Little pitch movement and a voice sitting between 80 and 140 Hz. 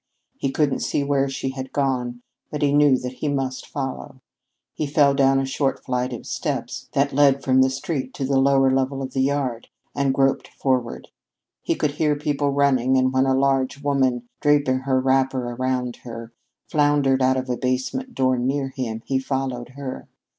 Yes: narrow, 1.4 semitones; low, 135 Hz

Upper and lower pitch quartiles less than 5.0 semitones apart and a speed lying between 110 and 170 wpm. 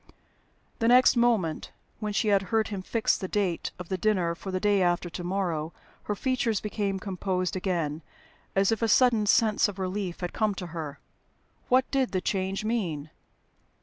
No: average, 3.2 semitones; average, 180 wpm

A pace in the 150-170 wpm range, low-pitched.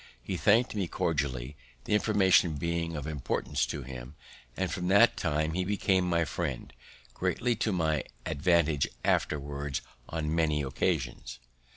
No: average, 140 wpm; very low, 80 Hz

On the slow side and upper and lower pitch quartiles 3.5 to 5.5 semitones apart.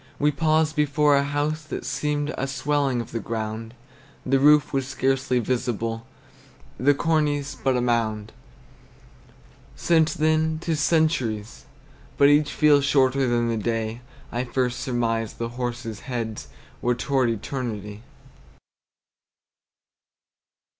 Yes: slow, 125 wpm; average, 4.0 semitones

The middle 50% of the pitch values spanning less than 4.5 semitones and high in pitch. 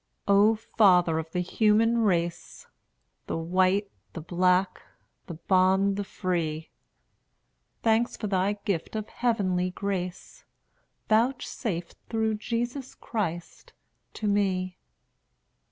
Yes: average, 3.4 semitones; high, 195 Hz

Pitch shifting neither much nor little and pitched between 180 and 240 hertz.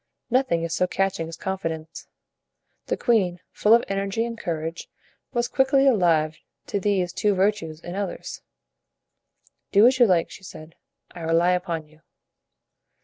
Yes: average, 4.2 semitones; medium, 185 Hz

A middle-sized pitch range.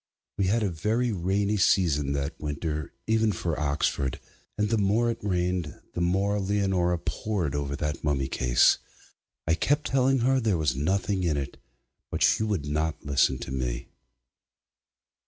No: wide, 6.0 semitones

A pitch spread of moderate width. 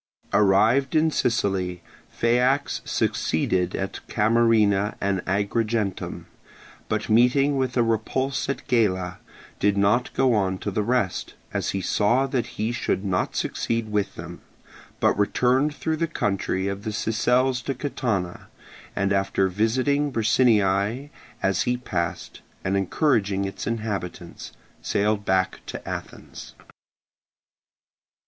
Yes: average, 4.1 semitones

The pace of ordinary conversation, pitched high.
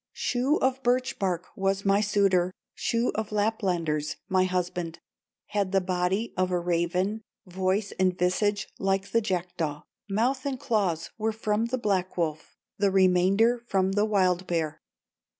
Yes: average, 150 wpm; high, 195 Hz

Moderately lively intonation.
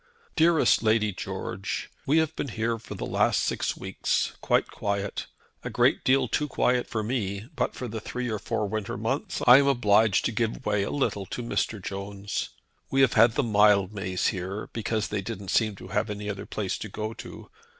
Yes: average, 3.0 semitones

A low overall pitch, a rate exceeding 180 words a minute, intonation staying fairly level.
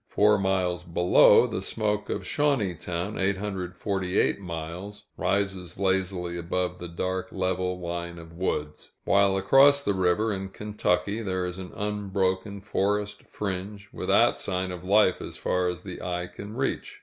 No: very low, 95 Hz; average, 145 wpm; narrow, 2.2 semitones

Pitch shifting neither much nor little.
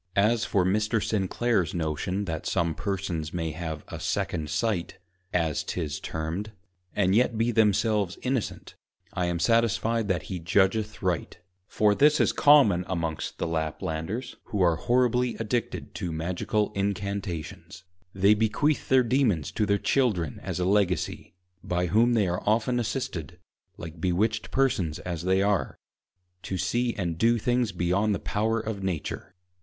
Yes: average, 4.4 semitones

